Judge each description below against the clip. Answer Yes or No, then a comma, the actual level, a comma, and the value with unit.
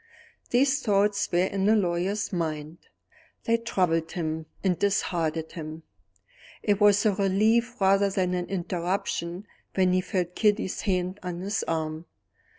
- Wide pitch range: No, average, 3.0 semitones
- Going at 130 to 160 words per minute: Yes, average, 140 wpm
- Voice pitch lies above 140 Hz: Yes, medium, 185 Hz